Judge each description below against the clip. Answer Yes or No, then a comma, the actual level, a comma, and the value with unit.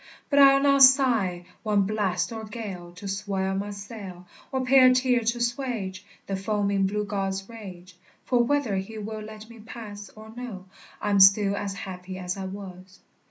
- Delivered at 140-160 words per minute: No, average, 175 wpm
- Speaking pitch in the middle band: No, high, 205 Hz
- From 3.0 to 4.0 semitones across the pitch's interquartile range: Yes, average, 3.3 semitones